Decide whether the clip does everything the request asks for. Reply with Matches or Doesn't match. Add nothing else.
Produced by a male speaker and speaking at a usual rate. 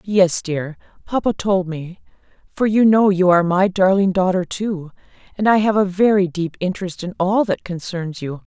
Doesn't match